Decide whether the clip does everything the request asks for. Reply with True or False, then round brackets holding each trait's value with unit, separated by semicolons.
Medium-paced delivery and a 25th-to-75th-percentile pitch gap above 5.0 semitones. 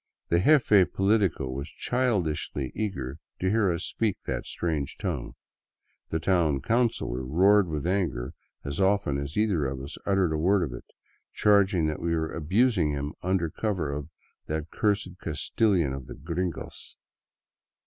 True (155 wpm; 5.4 semitones)